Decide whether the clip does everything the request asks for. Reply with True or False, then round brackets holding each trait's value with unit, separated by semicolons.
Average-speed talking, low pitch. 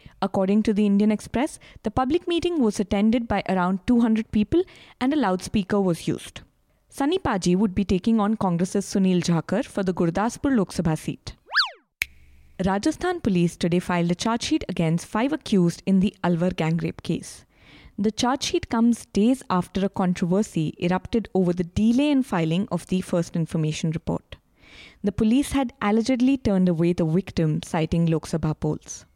False (165 wpm; 195 Hz)